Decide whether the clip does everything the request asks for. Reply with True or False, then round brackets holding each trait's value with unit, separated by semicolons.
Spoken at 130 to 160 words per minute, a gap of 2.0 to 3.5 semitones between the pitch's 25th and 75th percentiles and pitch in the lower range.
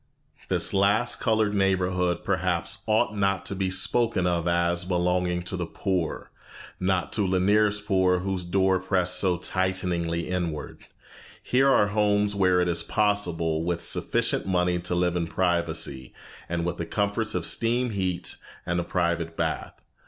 True (150 wpm; 2.4 semitones; 90 Hz)